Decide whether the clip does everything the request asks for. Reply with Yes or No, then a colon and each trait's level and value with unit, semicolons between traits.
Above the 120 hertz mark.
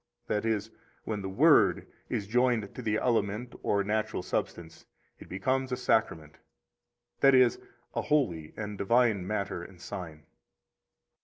No: low, 105 Hz